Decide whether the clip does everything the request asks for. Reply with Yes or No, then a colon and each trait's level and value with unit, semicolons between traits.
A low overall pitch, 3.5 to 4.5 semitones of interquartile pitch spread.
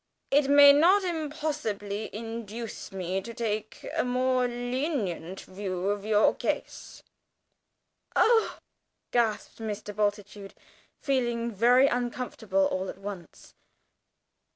No: high, 225 Hz; average, 4.1 semitones